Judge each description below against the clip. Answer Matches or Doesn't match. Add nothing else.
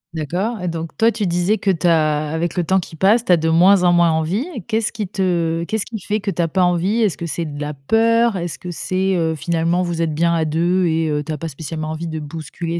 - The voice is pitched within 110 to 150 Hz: Doesn't match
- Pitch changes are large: Doesn't match